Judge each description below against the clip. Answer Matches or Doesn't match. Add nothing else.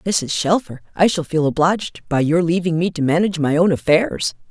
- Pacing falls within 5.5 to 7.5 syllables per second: Doesn't match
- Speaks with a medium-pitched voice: Matches